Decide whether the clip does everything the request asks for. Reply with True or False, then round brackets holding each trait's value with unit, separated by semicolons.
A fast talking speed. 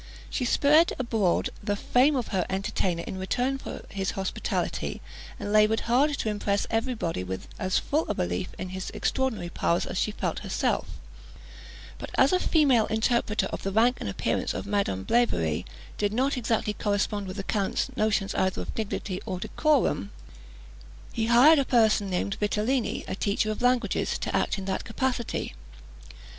False (170 wpm)